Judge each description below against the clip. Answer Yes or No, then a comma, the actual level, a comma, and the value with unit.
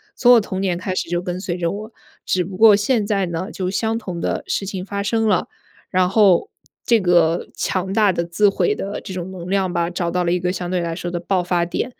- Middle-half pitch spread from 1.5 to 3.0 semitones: Yes, narrow, 2.6 semitones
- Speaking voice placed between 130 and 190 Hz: Yes, medium, 185 Hz